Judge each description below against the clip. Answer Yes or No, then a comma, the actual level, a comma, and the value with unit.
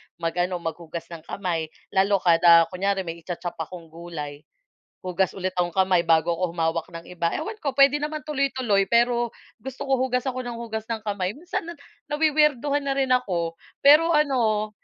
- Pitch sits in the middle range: No, high, 195 Hz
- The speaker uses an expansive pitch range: Yes, wide, 7.5 semitones